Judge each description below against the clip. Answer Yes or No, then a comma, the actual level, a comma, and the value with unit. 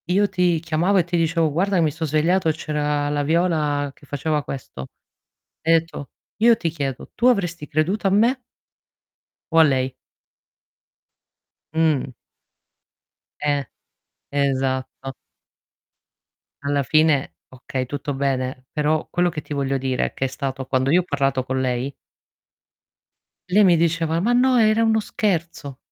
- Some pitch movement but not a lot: Yes, average, 4.0 semitones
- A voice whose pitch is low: No, medium, 155 Hz